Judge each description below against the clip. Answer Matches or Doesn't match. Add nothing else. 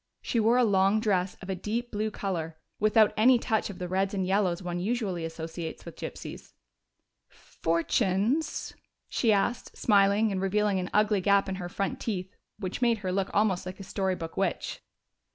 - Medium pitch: Doesn't match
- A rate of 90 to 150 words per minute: Doesn't match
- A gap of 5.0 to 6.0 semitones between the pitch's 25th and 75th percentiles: Doesn't match